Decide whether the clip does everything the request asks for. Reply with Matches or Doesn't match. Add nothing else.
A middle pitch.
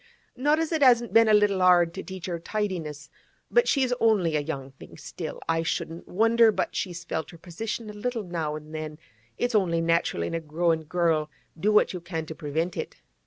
Matches